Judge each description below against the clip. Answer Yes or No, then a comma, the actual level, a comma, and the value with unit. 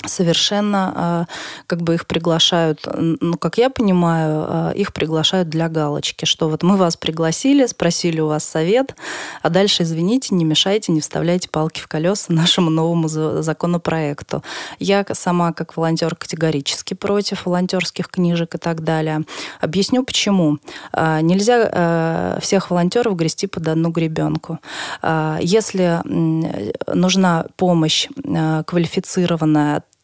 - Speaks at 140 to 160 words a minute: No, average, 120 wpm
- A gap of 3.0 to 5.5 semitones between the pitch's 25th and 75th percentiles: No, narrow, 2.6 semitones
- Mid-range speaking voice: Yes, medium, 170 Hz